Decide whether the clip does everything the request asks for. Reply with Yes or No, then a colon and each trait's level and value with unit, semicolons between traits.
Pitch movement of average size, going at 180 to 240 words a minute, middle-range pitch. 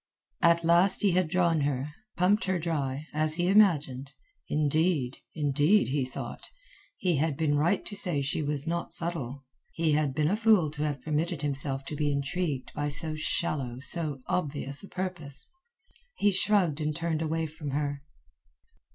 No: average, 3.3 semitones; average, 165 wpm; medium, 155 Hz